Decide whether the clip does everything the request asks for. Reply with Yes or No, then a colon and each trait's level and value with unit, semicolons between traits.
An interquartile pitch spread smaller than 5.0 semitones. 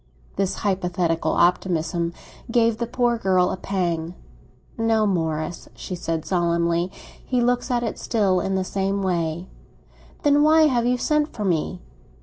No: average, 5.3 semitones